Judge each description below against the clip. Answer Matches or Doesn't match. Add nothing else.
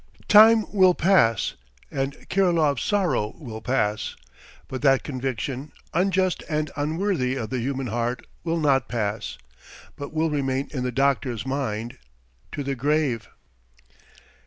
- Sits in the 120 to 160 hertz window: Matches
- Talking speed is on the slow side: Matches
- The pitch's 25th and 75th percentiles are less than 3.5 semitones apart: Doesn't match